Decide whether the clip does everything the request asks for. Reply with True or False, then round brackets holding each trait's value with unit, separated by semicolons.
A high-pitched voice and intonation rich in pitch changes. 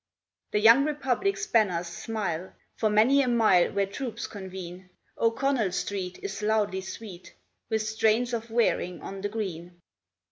False (215 Hz; 3.7 semitones)